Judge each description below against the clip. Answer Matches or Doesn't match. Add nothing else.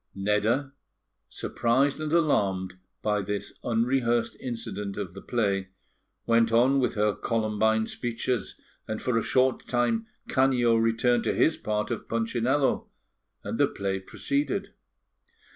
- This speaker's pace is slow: Matches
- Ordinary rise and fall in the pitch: Matches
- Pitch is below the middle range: Matches